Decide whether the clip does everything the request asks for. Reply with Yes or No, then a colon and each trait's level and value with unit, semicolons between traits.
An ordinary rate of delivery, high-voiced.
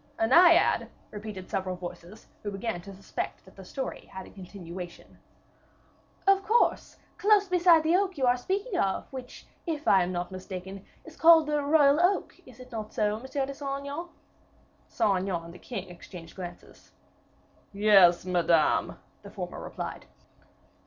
Yes: average, 160 wpm; high, 215 Hz